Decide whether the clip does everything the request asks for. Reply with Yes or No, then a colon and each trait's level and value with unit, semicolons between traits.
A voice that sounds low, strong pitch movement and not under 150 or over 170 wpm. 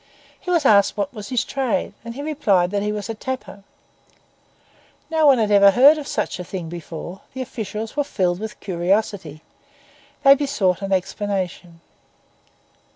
No: high, 205 Hz; wide, 5.7 semitones; average, 155 wpm